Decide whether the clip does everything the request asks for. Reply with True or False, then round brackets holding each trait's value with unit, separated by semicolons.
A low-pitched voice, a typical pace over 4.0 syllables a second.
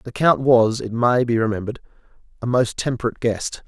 True (120 Hz; 5.8 syllables/s)